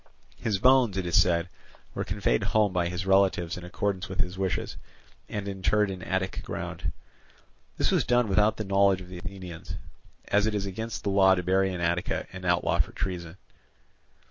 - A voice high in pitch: No, very low, 95 Hz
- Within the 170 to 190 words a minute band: Yes, average, 185 wpm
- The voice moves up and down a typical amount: No, narrow, 1.9 semitones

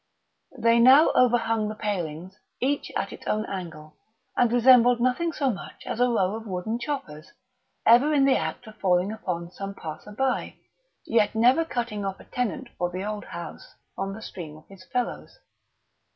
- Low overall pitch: No, high, 215 Hz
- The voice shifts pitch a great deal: No, average, 4.9 semitones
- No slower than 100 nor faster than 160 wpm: No, average, 175 wpm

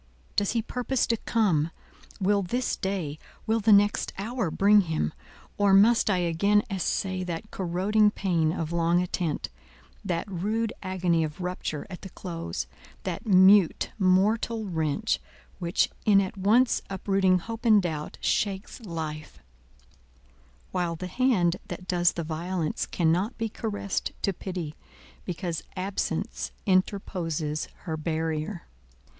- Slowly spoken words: Yes, slow, 125 wpm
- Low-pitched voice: No, medium, 185 Hz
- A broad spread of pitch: No, average, 3.6 semitones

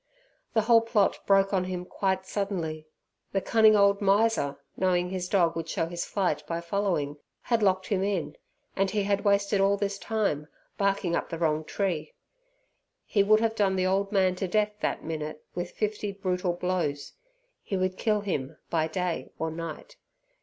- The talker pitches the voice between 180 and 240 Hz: Yes, high, 190 Hz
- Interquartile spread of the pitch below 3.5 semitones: Yes, average, 3.0 semitones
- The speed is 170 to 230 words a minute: Yes, average, 175 wpm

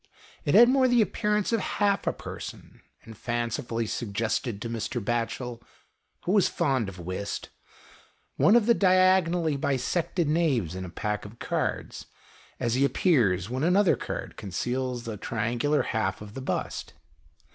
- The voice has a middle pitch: No, low, 125 Hz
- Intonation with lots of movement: Yes, wide, 8.1 semitones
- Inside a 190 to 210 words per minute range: No, average, 150 wpm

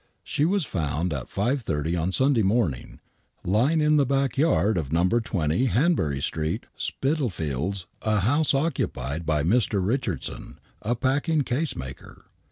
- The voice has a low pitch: Yes, low, 110 Hz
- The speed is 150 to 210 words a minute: No, average, 140 wpm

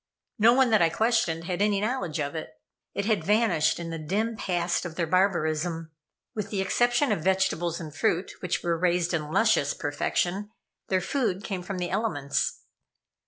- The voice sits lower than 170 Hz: No, medium, 180 Hz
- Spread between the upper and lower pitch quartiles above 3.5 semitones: Yes, average, 4.1 semitones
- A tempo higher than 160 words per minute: Yes, average, 175 wpm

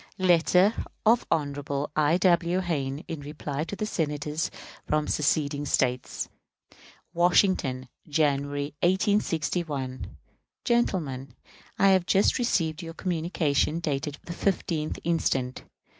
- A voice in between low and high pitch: Yes, medium, 160 Hz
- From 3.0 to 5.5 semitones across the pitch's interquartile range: Yes, average, 3.7 semitones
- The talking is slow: Yes, slow, 100 wpm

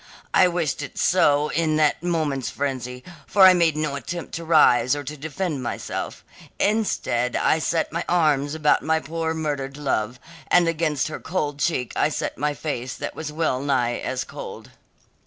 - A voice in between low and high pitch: Yes, medium, 150 Hz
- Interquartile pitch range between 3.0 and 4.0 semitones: Yes, average, 3.3 semitones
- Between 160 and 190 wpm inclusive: Yes, average, 175 wpm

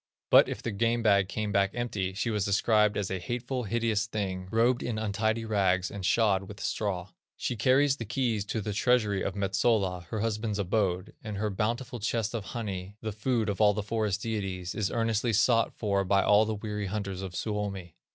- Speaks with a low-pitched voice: Yes, low, 105 Hz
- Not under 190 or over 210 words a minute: Yes, average, 200 wpm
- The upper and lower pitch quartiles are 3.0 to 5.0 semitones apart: No, narrow, 2.6 semitones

